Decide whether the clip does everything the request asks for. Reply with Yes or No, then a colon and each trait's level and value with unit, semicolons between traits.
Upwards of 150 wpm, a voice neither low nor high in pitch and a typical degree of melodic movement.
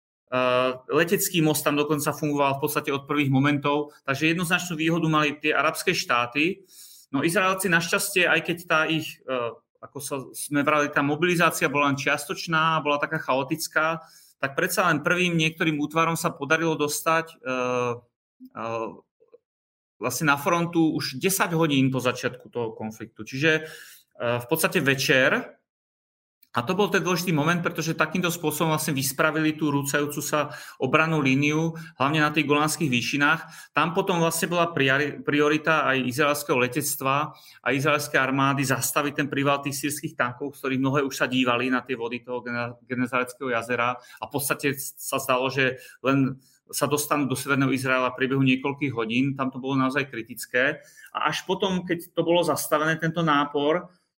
Yes: average, 160 wpm; medium, 150 Hz; average, 3.4 semitones